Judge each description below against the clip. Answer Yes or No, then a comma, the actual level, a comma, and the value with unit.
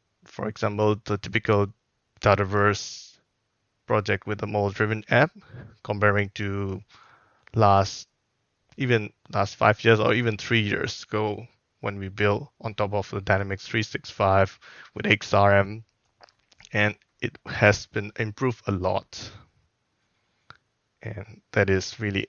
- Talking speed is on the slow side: Yes, slow, 120 wpm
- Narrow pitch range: Yes, narrow, 2.0 semitones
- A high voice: No, low, 105 Hz